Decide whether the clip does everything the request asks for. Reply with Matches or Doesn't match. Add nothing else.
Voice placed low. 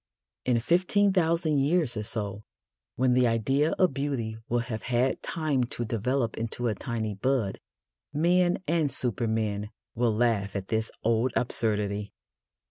Matches